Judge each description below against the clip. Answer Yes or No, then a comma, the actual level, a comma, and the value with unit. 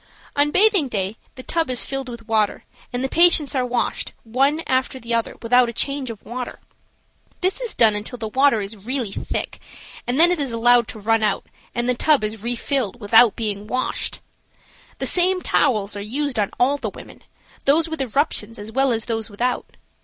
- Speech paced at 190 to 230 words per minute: Yes, average, 195 wpm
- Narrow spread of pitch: No, average, 4.0 semitones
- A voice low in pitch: No, high, 245 Hz